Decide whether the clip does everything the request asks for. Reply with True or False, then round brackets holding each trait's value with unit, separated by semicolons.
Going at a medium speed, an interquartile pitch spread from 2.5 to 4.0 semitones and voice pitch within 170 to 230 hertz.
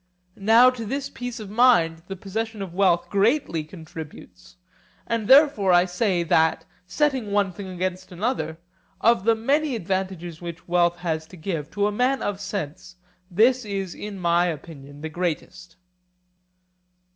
False (150 wpm; 4.6 semitones; 190 Hz)